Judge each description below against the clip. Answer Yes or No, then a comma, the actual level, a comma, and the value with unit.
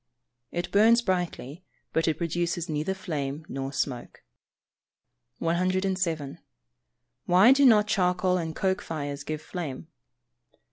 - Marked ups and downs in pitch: No, average, 3.5 semitones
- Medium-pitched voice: Yes, medium, 175 Hz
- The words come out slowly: Yes, slow, 120 wpm